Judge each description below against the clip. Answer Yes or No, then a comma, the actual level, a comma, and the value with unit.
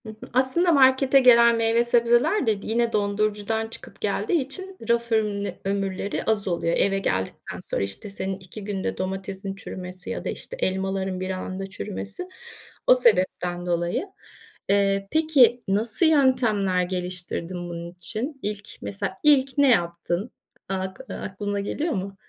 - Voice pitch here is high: Yes, high, 205 Hz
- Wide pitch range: No, average, 4.2 semitones